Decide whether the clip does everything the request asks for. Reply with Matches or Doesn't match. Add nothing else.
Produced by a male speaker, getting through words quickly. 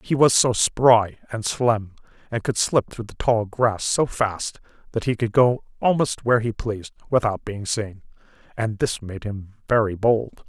Doesn't match